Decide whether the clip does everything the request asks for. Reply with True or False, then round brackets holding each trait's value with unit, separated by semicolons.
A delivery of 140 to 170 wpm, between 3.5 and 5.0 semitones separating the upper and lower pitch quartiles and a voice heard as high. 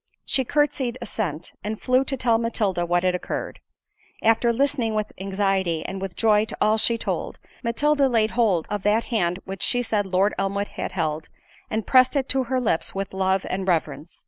False (190 wpm; 3.9 semitones; 210 Hz)